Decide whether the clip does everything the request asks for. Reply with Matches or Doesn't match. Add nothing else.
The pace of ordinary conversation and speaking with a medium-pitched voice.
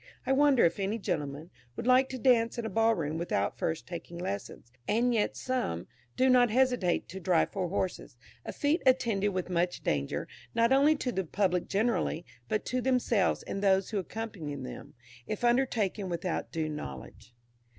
Doesn't match